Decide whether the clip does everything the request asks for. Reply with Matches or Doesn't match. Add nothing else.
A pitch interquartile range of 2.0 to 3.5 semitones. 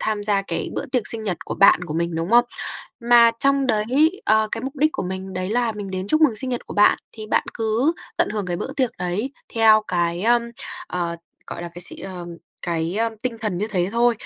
Doesn't match